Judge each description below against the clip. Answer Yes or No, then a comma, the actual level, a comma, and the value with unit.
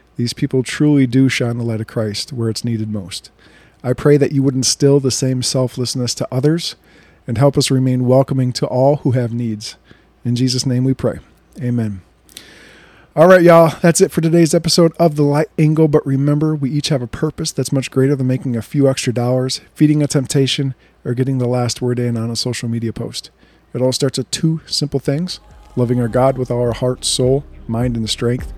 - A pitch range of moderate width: Yes, average, 3.1 semitones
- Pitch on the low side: Yes, low, 130 Hz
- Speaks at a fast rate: Yes, fast, 210 wpm